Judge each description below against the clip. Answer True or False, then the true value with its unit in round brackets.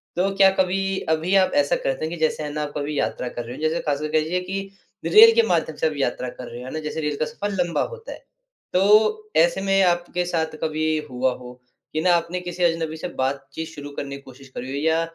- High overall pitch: False (160 Hz)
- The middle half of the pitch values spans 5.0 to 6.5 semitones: False (4.2 semitones)